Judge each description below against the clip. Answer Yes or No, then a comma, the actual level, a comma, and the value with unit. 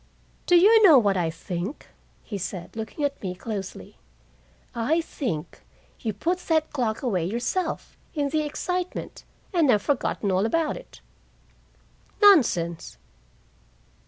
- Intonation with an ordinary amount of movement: No, wide, 8.9 semitones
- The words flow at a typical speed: No, slow, 130 wpm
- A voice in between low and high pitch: No, high, 245 Hz